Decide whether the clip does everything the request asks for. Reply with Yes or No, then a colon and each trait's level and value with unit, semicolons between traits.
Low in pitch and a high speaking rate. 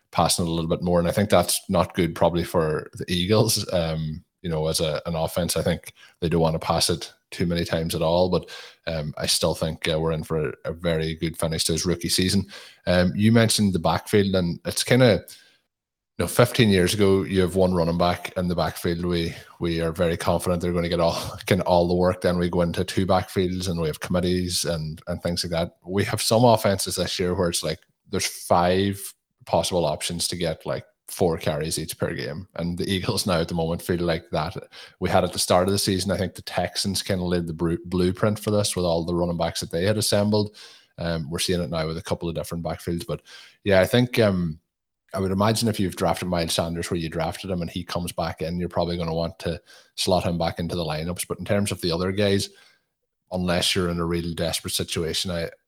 Yes: very low, 90 Hz; fast, 240 wpm